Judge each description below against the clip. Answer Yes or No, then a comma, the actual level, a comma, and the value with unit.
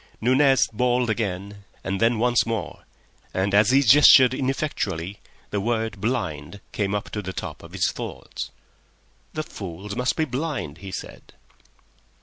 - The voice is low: Yes, low, 110 Hz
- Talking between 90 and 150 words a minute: Yes, average, 145 wpm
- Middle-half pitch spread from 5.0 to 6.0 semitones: No, average, 4.3 semitones